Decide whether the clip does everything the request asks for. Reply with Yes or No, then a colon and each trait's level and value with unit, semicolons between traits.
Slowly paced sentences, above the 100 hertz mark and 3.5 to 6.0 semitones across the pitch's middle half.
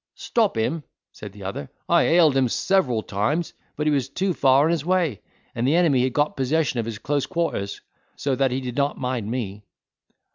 No: fast, 205 wpm; low, 135 Hz; wide, 5.4 semitones